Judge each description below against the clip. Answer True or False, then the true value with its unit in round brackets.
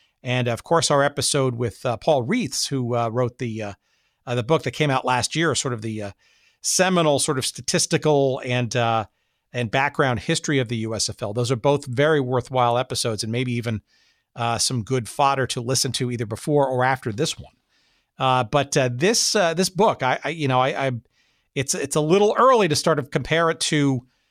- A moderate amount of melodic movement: True (3.5 semitones)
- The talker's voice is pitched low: True (130 Hz)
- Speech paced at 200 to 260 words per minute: True (205 wpm)